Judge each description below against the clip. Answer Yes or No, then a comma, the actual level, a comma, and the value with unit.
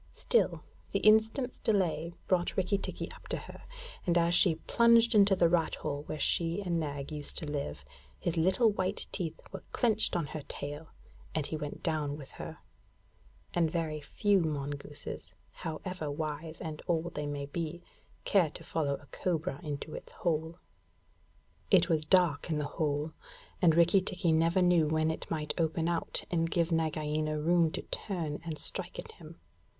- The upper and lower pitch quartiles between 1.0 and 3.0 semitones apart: Yes, average, 2.7 semitones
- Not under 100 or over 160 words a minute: No, average, 170 wpm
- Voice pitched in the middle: Yes, medium, 165 Hz